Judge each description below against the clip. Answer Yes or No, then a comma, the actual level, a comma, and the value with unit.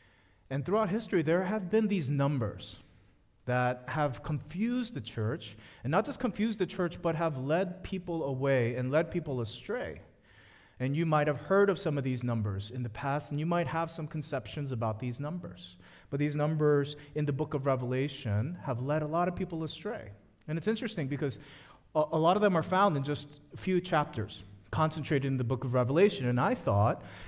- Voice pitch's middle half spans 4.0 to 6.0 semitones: Yes, average, 5.1 semitones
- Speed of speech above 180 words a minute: Yes, average, 195 wpm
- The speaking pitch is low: No, medium, 145 Hz